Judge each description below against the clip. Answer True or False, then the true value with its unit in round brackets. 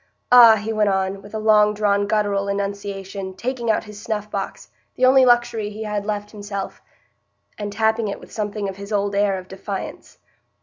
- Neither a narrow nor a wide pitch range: False (1.5 semitones)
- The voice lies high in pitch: True (205 Hz)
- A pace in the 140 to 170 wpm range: False (185 wpm)